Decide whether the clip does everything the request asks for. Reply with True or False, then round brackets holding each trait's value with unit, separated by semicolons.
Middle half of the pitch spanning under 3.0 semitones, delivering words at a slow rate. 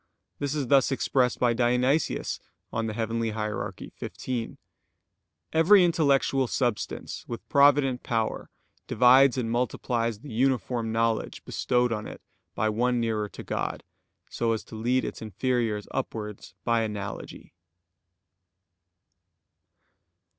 True (2.6 semitones; 110 wpm)